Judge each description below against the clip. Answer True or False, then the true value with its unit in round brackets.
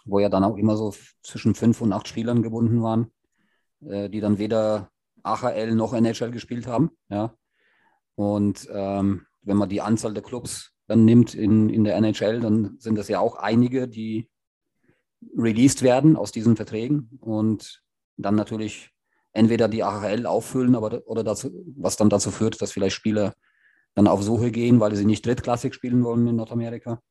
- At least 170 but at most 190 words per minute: True (175 wpm)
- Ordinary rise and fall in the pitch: False (2.1 semitones)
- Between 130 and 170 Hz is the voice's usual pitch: False (110 Hz)